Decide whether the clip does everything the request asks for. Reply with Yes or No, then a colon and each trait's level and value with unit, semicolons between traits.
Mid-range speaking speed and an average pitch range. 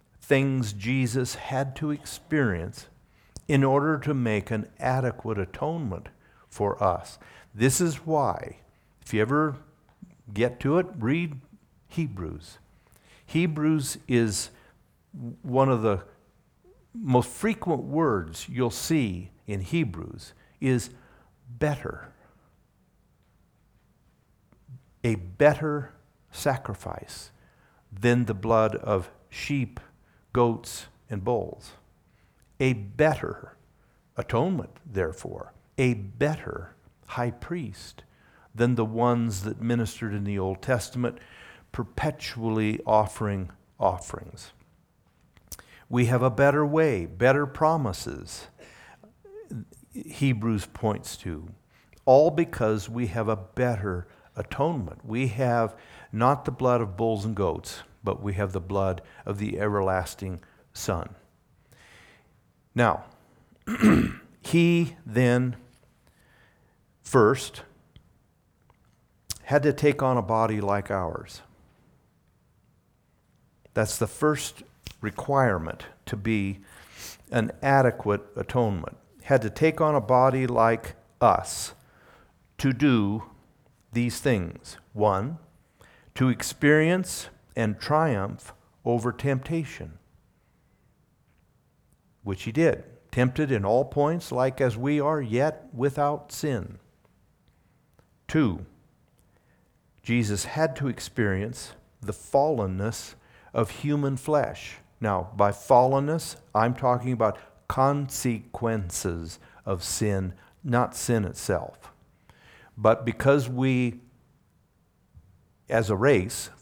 No: slow, 95 wpm; average, 4.8 semitones